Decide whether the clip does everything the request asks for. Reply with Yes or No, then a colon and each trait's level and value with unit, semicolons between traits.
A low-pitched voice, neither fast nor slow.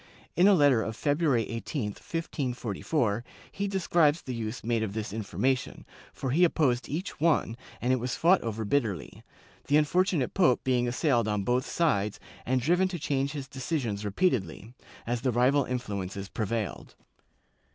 Yes: low, 125 Hz; average, 155 wpm